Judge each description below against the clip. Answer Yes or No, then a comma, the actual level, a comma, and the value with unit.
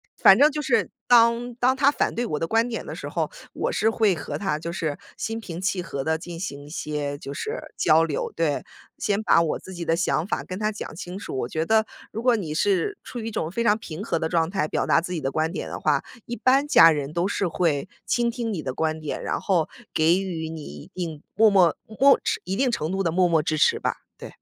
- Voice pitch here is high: No, medium, 180 Hz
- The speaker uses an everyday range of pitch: No, wide, 5.8 semitones